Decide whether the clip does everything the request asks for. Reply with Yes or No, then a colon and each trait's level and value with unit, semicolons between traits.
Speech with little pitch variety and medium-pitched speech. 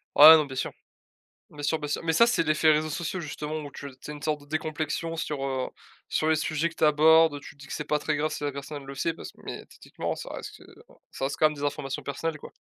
Yes: narrow, 1.5 semitones; medium, 150 Hz